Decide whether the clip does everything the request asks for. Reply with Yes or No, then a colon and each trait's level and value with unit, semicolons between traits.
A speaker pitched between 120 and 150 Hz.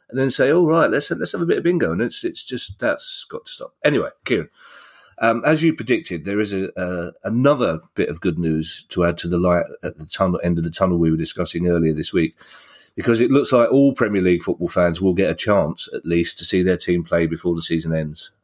No: very low, 90 Hz